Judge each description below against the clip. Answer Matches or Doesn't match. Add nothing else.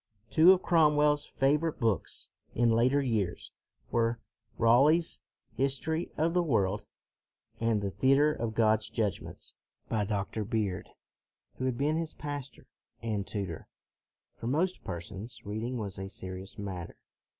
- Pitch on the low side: Matches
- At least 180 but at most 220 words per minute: Doesn't match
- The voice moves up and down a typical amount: Doesn't match